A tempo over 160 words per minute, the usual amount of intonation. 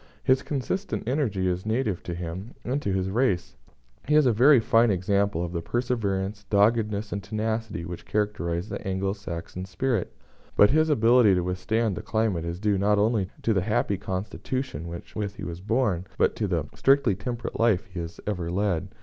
Yes: average, 185 wpm; average, 3.9 semitones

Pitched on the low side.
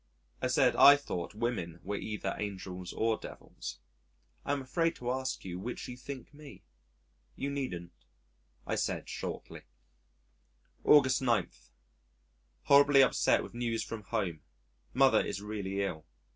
Yes: low, 115 Hz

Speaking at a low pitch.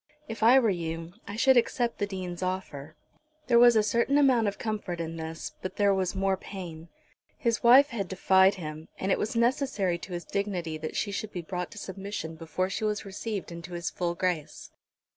No: high, 190 Hz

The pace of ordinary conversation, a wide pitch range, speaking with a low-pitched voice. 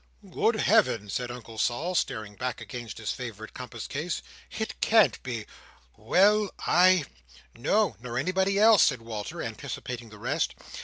Yes: average, 145 wpm; wide, 8.3 semitones; low, 125 Hz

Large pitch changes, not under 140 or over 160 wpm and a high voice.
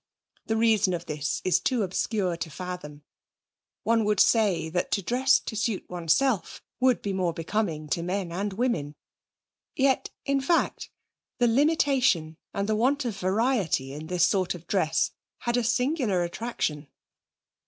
Yes: wide, 5.9 semitones; average, 155 wpm; high, 200 Hz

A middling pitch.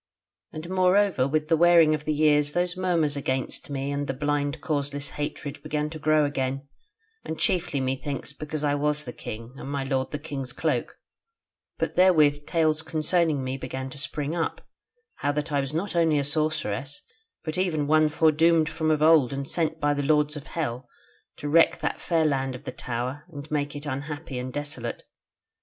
Yes: medium, 150 Hz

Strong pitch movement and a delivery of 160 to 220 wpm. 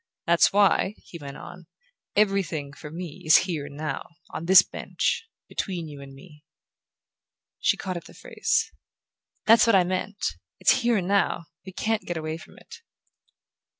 No: average, 4.1 semitones; average, 165 wpm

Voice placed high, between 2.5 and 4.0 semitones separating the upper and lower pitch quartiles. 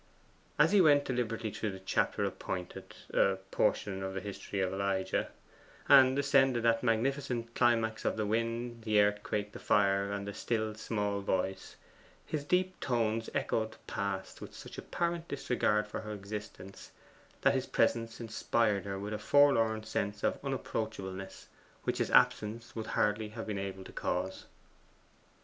No: low, 110 Hz; average, 2.9 semitones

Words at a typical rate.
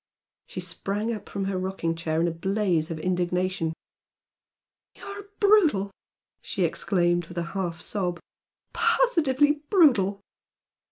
No: slow, 125 wpm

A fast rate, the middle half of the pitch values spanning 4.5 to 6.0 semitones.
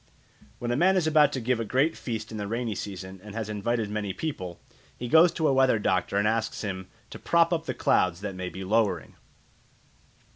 Yes: fast, 215 wpm; average, 5.1 semitones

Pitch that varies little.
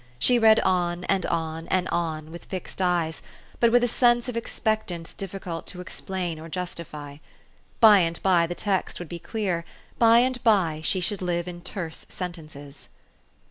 No: average, 3.7 semitones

